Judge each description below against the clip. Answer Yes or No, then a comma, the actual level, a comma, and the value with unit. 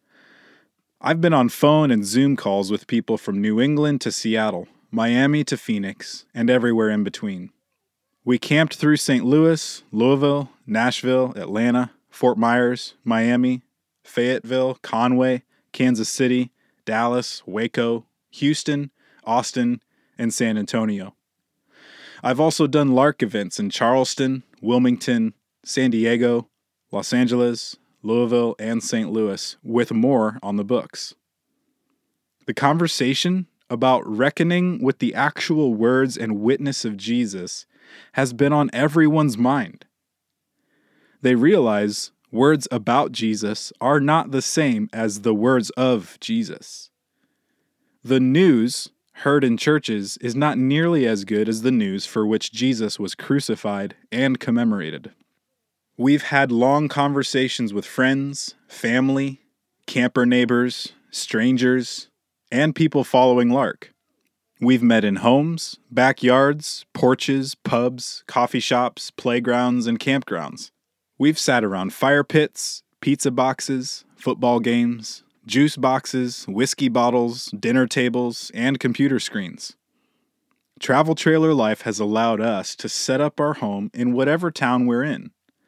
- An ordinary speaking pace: No, slow, 125 wpm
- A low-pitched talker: Yes, low, 125 Hz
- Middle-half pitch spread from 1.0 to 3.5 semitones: Yes, average, 3.1 semitones